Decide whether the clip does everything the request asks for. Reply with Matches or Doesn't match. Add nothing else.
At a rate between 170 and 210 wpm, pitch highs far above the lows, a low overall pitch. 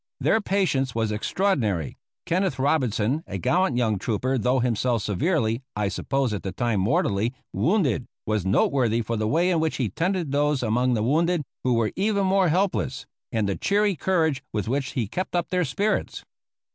Matches